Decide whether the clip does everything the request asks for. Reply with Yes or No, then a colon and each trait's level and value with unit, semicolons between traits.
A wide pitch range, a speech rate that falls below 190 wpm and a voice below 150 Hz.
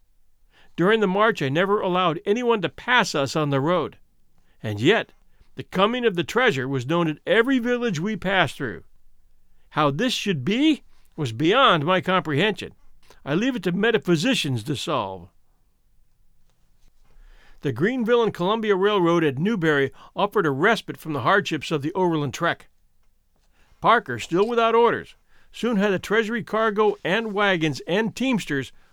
No: wide, 6.6 semitones; average, 150 wpm; medium, 185 Hz